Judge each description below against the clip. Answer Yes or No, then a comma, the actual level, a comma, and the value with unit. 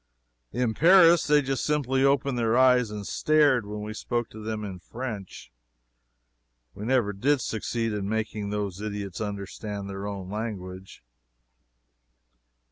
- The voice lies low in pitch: Yes, low, 110 Hz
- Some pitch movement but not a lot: Yes, average, 4.2 semitones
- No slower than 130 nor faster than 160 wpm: Yes, slow, 135 wpm